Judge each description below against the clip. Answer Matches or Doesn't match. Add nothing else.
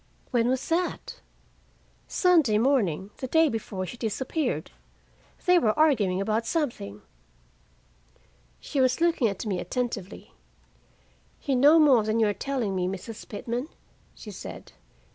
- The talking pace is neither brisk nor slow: Doesn't match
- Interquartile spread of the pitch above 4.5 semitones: Matches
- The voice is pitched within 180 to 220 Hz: Doesn't match